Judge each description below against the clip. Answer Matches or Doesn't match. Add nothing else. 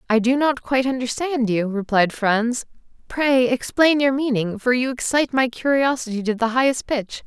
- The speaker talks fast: Doesn't match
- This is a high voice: Matches